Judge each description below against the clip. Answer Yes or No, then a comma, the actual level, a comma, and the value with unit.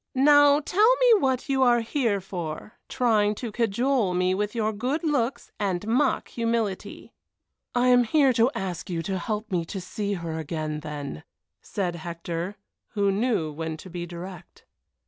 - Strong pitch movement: Yes, wide, 6.0 semitones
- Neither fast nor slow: Yes, average, 165 wpm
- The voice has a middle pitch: No, high, 210 Hz